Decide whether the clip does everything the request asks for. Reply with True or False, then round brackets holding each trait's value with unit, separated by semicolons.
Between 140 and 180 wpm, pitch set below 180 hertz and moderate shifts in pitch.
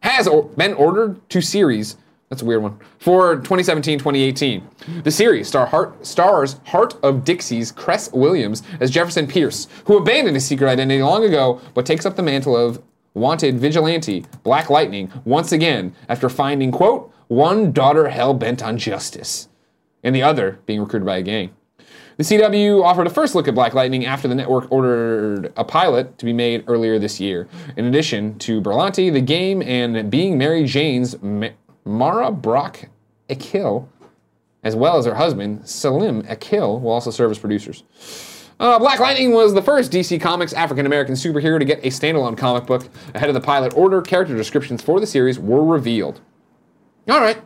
False (175 wpm; 135 Hz; 6.1 semitones)